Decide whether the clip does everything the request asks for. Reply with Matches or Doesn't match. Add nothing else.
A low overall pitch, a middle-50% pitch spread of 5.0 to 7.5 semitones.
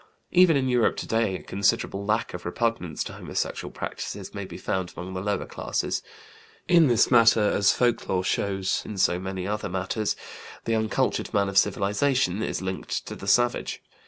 Doesn't match